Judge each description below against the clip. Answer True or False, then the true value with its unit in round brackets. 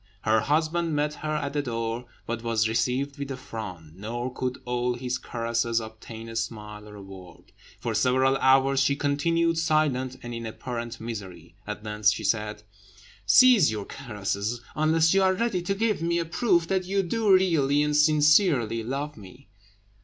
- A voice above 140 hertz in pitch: False (130 Hz)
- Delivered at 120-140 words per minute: False (175 wpm)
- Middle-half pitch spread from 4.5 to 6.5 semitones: True (5.4 semitones)